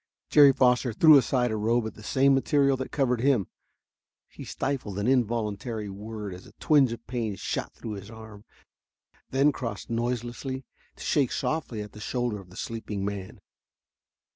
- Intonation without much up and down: No, average, 3.9 semitones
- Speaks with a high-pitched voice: No, low, 120 Hz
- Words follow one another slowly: No, average, 165 wpm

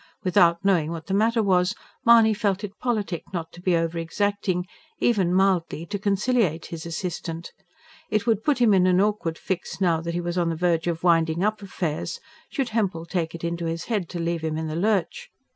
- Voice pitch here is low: No, medium, 180 Hz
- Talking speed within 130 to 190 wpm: No, fast, 205 wpm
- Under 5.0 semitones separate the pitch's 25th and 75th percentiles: Yes, average, 3.6 semitones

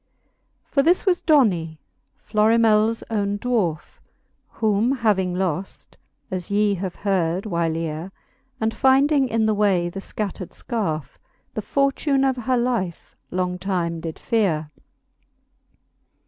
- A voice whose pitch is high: Yes, high, 205 Hz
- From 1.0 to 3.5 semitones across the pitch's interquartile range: No, average, 4.8 semitones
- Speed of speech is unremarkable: No, slow, 120 wpm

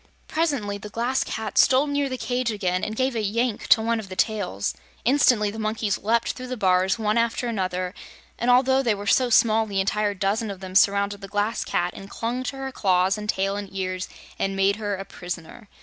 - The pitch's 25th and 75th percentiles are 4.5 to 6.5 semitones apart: No, average, 3.4 semitones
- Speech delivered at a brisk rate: Yes, fast, 215 wpm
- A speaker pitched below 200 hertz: No, high, 210 Hz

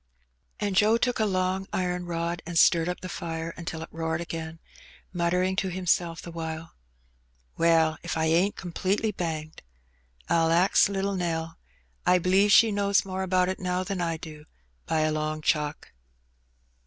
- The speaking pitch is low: No, medium, 175 Hz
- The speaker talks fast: No, average, 165 wpm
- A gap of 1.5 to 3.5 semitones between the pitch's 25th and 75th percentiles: Yes, narrow, 2.4 semitones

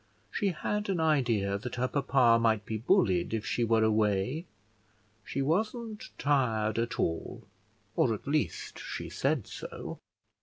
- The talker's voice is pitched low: Yes, low, 125 Hz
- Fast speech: No, average, 145 wpm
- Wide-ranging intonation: Yes, wide, 5.8 semitones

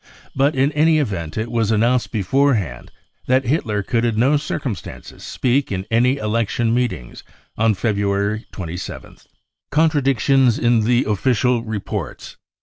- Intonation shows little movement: No, average, 3.9 semitones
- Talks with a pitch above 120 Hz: No, low, 115 Hz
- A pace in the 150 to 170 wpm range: No, average, 140 wpm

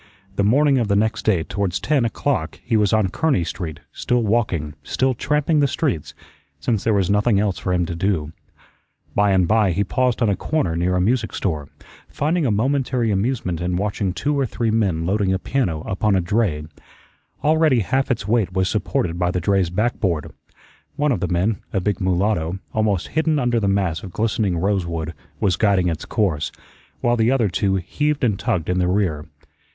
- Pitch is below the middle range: Yes, low, 100 Hz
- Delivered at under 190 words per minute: No, average, 195 wpm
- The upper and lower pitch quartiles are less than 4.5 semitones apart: No, average, 4.8 semitones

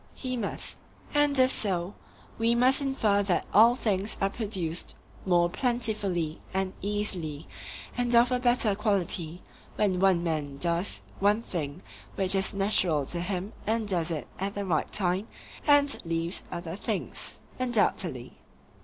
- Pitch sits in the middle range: No, high, 195 Hz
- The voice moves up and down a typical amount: Yes, average, 4.7 semitones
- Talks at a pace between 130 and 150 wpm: Yes, average, 145 wpm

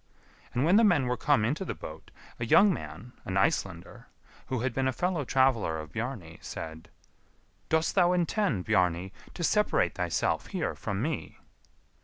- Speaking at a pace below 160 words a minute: No, average, 165 wpm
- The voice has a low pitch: Yes, low, 130 Hz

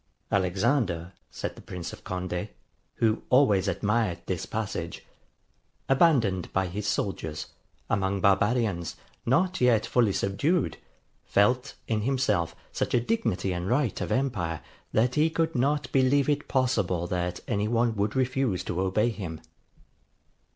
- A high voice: No, low, 105 Hz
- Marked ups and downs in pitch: Yes, wide, 5.7 semitones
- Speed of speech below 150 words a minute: Yes, slow, 135 wpm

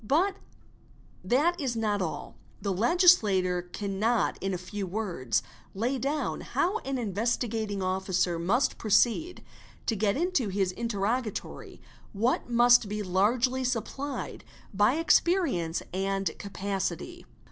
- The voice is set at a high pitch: Yes, high, 215 Hz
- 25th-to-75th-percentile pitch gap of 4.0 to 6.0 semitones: Yes, average, 5.0 semitones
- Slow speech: Yes, slow, 115 wpm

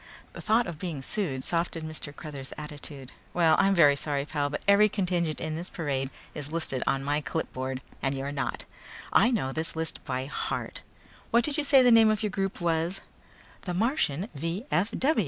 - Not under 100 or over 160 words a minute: No, average, 185 wpm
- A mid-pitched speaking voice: Yes, medium, 160 Hz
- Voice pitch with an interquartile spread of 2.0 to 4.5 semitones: No, wide, 5.4 semitones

